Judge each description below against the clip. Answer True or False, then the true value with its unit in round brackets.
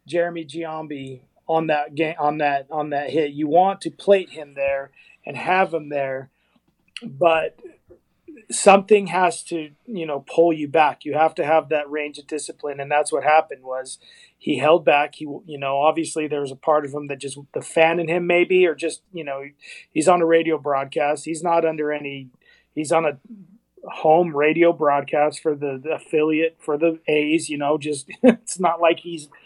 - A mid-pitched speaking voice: True (155 Hz)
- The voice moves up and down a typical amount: False (2.3 semitones)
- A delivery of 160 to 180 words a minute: False (195 wpm)